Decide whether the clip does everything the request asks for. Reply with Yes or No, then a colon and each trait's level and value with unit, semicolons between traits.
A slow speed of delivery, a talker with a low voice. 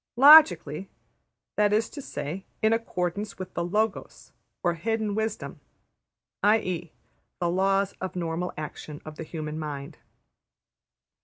No: slow, 125 wpm; medium, 185 Hz